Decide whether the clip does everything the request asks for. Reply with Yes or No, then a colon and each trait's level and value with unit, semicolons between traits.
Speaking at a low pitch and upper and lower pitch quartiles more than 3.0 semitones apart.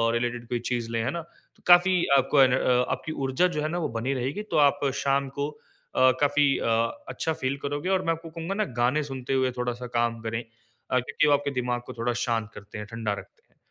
Yes: low, 130 Hz; average, 3.6 semitones